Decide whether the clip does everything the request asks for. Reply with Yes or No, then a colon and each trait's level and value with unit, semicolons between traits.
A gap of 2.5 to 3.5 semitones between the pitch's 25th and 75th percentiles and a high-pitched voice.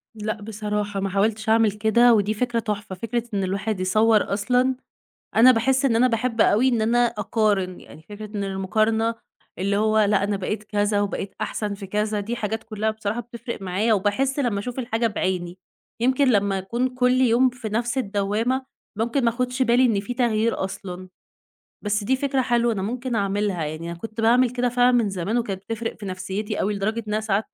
Yes: average, 2.9 semitones; high, 220 Hz